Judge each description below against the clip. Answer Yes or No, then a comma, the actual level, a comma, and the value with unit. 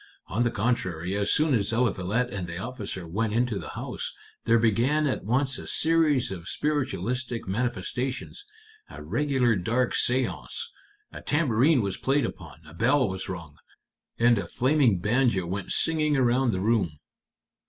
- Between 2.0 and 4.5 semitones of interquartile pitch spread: No, average, 4.9 semitones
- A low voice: Yes, low, 120 Hz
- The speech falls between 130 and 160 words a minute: Yes, average, 155 wpm